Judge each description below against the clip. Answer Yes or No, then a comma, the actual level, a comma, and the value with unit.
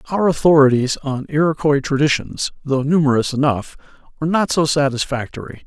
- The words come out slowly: Yes, slow, 125 wpm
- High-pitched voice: No, medium, 145 Hz